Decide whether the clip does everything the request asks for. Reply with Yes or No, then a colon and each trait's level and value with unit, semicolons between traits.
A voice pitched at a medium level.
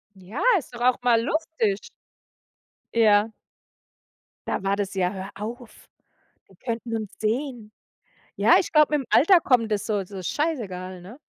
No: high, 220 Hz